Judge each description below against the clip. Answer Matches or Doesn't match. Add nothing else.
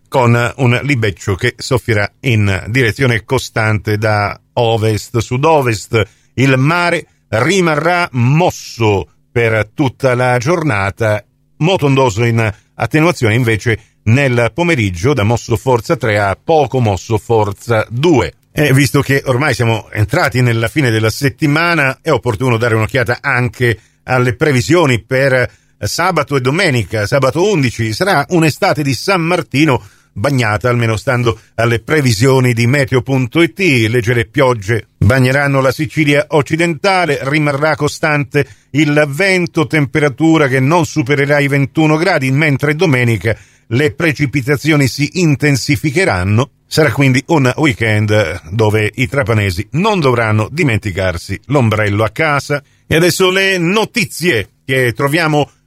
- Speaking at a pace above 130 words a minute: Doesn't match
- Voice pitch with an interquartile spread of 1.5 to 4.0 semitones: Doesn't match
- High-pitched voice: Doesn't match